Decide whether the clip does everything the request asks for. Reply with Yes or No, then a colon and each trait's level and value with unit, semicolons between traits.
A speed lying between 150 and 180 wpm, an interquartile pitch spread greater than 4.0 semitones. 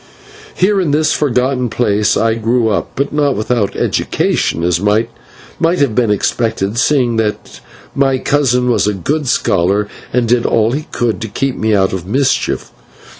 Yes: average, 165 wpm; average, 4.4 semitones